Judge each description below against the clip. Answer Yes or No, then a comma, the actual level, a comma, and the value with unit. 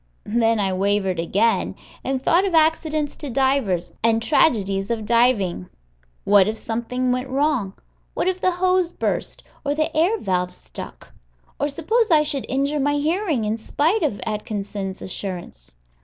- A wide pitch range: Yes, wide, 7.2 semitones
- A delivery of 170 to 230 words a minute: No, average, 155 wpm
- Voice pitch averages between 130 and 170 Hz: No, high, 245 Hz